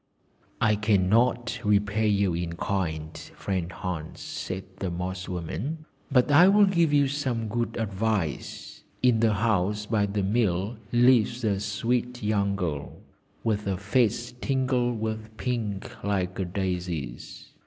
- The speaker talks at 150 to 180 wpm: No, slow, 135 wpm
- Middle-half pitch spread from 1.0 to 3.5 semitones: No, average, 4.3 semitones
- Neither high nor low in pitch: No, low, 105 Hz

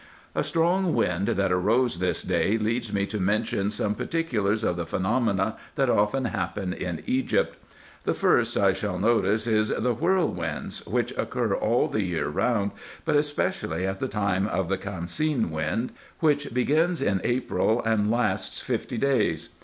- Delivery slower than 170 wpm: Yes, average, 160 wpm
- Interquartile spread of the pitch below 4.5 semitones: No, average, 4.8 semitones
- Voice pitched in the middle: No, low, 105 Hz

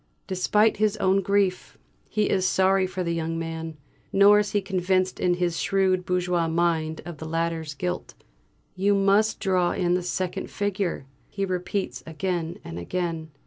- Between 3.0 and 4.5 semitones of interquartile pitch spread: No, narrow, 2.6 semitones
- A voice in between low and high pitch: Yes, medium, 180 Hz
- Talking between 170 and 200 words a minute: No, average, 160 wpm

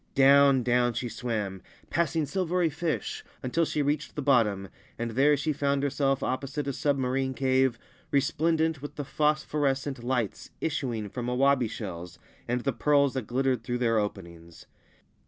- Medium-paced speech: Yes, average, 150 wpm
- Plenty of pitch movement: No, average, 3.3 semitones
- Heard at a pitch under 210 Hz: Yes, low, 135 Hz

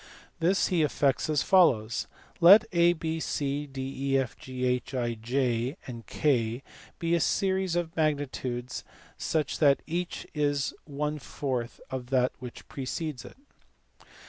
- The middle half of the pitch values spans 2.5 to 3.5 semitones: No, average, 4.2 semitones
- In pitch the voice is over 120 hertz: Yes, medium, 140 Hz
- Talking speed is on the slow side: Yes, slow, 115 wpm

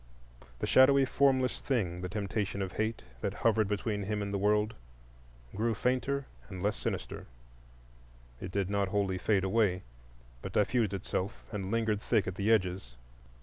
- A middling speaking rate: Yes, average, 150 wpm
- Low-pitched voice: Yes, low, 100 Hz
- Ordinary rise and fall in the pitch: Yes, average, 3.1 semitones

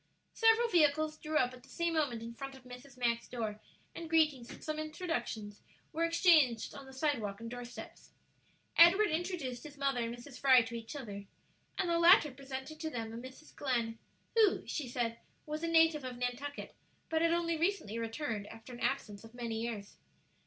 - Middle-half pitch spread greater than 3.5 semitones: Yes, average, 5.2 semitones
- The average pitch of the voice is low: No, very high, 265 Hz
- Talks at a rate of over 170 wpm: Yes, average, 190 wpm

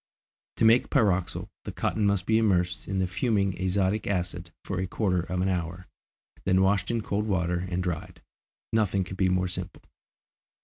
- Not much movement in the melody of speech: Yes, narrow, 2.1 semitones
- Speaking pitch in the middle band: No, very low, 95 Hz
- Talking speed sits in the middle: Yes, average, 175 wpm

